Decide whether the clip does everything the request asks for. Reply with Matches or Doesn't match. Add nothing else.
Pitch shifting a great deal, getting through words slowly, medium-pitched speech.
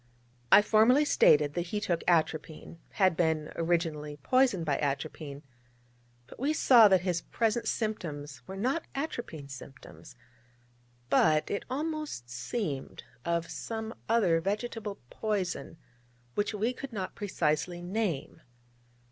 Matches